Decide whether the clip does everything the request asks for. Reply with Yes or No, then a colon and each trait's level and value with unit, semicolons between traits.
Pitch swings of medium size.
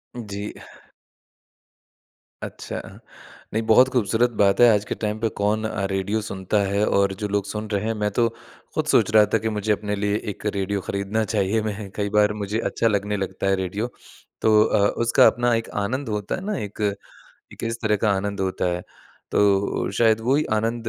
No: narrow, 2.0 semitones